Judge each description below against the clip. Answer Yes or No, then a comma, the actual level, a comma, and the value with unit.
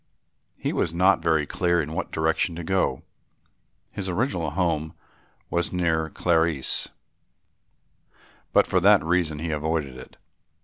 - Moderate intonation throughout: No, narrow, 2.2 semitones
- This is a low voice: Yes, very low, 85 Hz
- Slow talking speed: Yes, slow, 130 wpm